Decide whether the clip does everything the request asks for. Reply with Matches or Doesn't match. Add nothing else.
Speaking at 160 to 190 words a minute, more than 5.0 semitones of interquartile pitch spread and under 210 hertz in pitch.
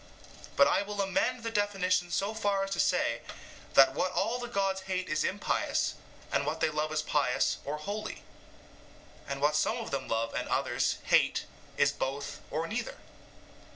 Matches